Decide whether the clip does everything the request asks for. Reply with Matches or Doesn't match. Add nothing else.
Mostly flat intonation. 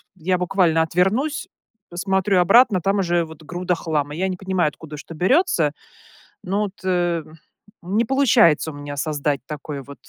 Doesn't match